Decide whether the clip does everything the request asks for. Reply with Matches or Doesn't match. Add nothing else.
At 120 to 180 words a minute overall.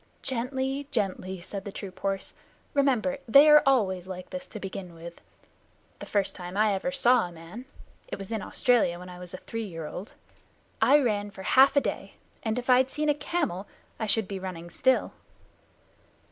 Doesn't match